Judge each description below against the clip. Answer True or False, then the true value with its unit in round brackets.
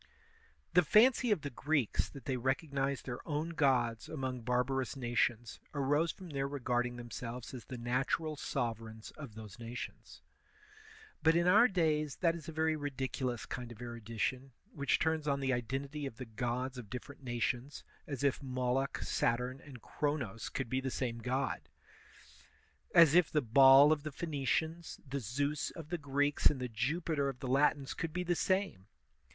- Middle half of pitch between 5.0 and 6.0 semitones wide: False (3.6 semitones)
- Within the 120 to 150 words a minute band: False (170 wpm)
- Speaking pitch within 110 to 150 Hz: True (135 Hz)